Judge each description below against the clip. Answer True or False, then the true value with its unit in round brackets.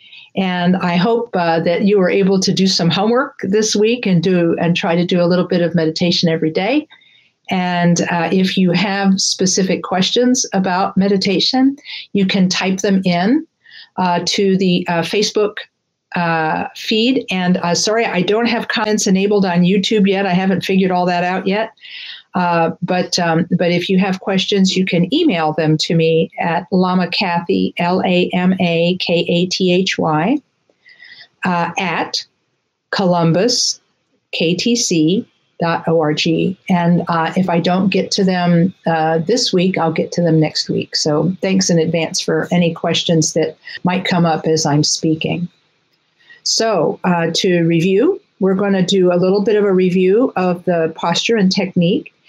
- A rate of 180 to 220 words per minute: False (165 wpm)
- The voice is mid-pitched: True (180 Hz)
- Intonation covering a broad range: False (2.6 semitones)